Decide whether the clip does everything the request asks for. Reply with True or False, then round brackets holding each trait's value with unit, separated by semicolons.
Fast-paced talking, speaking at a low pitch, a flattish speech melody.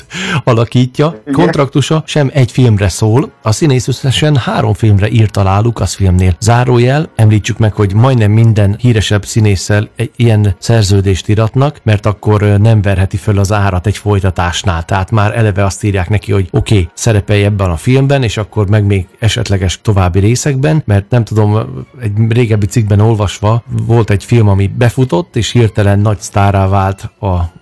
False (160 wpm; 110 Hz; 3.2 semitones)